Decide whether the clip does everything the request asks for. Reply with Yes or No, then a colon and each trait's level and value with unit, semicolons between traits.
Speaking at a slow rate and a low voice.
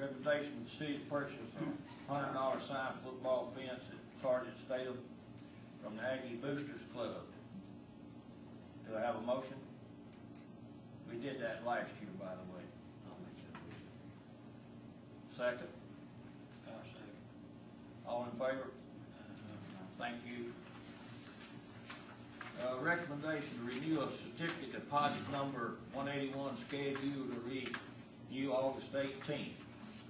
Yes: slow, 105 wpm; low, 125 Hz